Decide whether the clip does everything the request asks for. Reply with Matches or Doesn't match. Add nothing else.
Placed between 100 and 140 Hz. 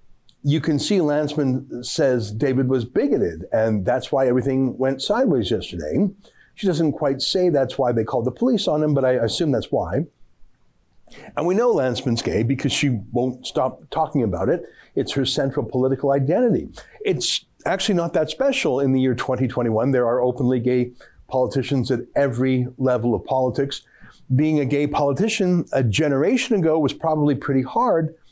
Matches